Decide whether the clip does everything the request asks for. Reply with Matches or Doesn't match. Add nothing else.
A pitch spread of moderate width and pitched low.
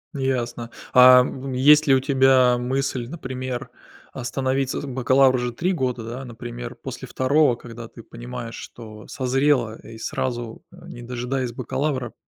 Doesn't match